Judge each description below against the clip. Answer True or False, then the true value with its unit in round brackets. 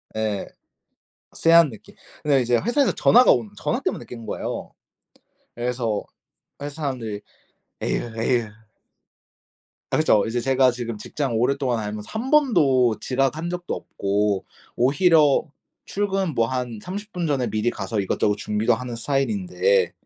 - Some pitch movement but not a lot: False (6.2 semitones)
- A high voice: False (125 Hz)